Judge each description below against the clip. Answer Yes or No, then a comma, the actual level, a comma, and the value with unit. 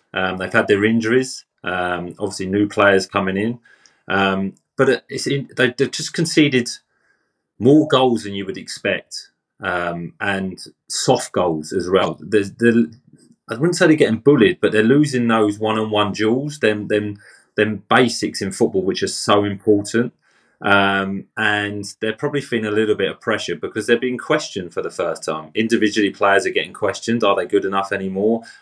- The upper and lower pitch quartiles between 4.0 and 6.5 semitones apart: No, average, 3.3 semitones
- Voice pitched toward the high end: No, low, 105 Hz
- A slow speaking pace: No, average, 165 wpm